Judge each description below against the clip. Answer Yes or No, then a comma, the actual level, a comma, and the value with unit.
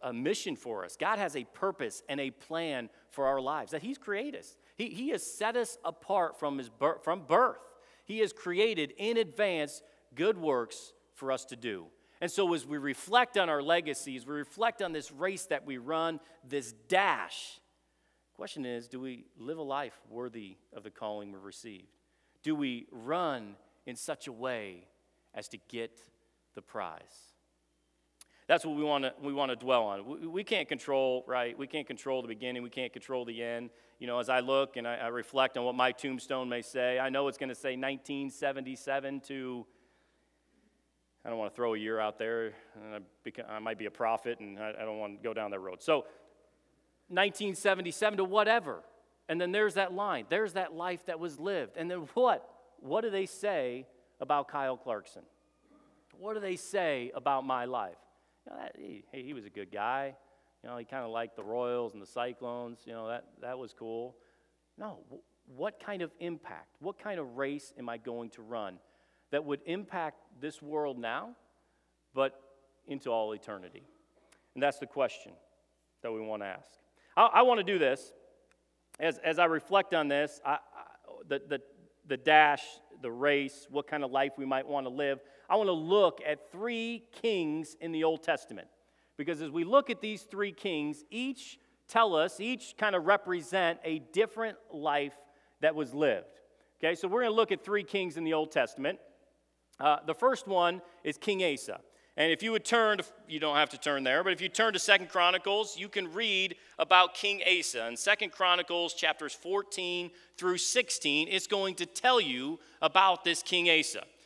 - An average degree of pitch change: No, wide, 7.1 semitones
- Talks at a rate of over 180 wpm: Yes, average, 195 wpm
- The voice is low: No, medium, 150 Hz